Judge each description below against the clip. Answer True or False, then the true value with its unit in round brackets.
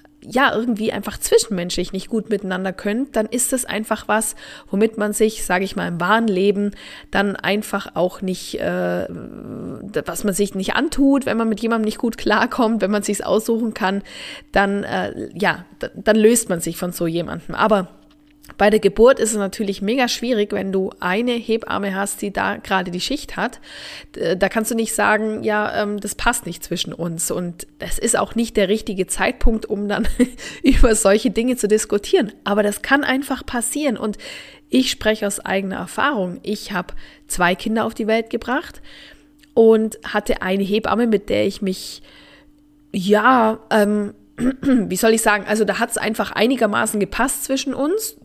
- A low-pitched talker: False (215 Hz)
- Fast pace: False (180 wpm)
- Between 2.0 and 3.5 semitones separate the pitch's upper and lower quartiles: True (3.0 semitones)